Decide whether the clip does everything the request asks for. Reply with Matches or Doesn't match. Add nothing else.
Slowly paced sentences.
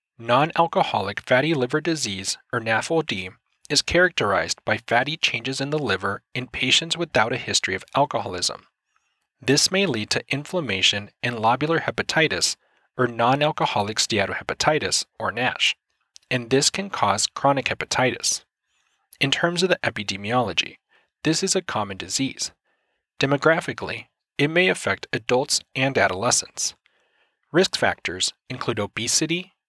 Matches